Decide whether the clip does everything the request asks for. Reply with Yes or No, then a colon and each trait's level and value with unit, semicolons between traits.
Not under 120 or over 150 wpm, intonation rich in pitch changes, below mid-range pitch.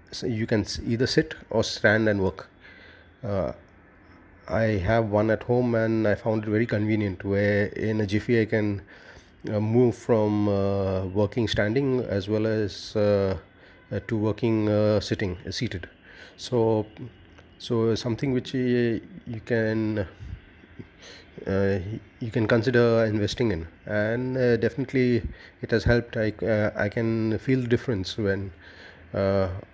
No: average, 145 wpm; average, 2.9 semitones; low, 105 Hz